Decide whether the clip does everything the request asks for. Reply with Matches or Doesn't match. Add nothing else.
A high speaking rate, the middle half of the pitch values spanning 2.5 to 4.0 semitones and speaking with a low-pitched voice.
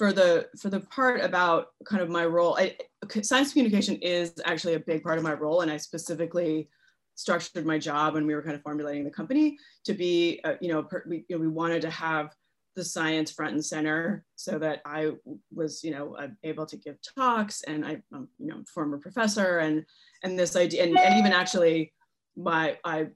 Doesn't match